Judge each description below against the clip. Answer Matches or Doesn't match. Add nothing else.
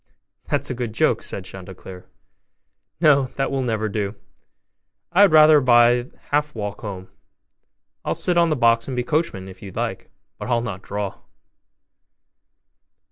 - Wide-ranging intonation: Matches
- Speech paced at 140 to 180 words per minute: Matches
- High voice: Doesn't match